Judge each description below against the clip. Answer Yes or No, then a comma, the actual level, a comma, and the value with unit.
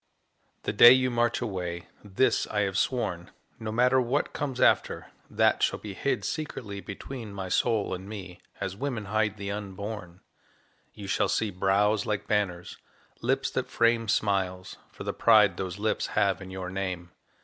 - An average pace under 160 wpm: No, average, 165 wpm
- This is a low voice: Yes, low, 105 Hz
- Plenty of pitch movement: No, average, 3.1 semitones